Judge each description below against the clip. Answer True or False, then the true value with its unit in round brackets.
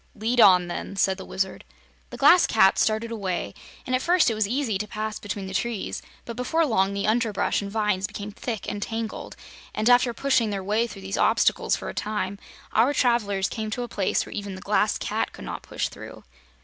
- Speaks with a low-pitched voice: False (215 Hz)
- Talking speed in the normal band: False (215 wpm)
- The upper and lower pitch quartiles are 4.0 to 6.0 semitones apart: False (3.1 semitones)